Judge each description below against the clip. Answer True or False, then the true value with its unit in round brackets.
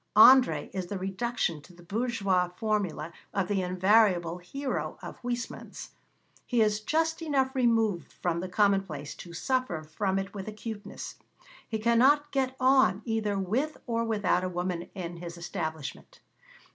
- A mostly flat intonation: False (4.9 semitones)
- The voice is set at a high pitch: True (205 Hz)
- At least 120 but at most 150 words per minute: True (145 wpm)